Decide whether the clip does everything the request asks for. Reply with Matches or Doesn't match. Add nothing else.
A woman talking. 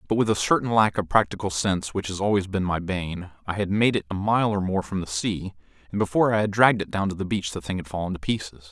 Doesn't match